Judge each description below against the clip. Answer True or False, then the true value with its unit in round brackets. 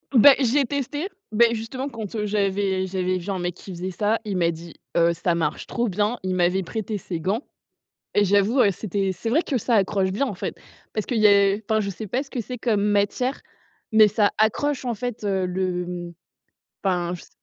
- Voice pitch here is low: False (205 Hz)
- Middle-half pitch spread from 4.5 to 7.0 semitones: False (3.7 semitones)